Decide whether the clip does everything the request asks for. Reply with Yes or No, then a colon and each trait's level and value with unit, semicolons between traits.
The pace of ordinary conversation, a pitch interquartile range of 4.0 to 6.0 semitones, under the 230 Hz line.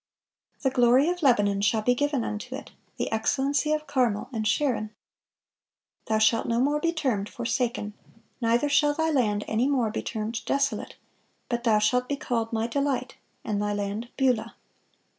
No: average, 165 wpm; average, 4.4 semitones; high, 240 Hz